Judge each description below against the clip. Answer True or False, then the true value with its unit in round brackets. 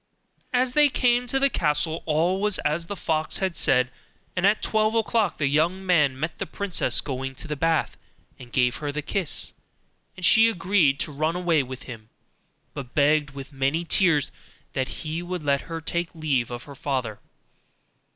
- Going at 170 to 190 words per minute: True (180 wpm)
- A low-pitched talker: False (155 Hz)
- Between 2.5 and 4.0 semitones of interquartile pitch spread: False (5.0 semitones)